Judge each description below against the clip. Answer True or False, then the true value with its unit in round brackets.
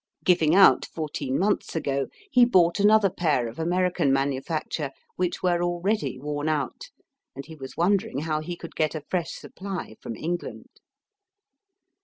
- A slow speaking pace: False (150 wpm)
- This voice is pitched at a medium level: True (165 Hz)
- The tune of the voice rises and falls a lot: False (3.8 semitones)